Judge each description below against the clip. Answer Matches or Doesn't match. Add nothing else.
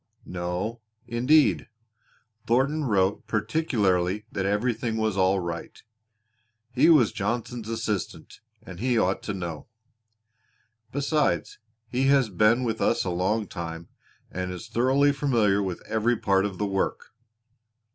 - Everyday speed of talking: Doesn't match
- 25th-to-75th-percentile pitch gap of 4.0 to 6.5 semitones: Matches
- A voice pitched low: Matches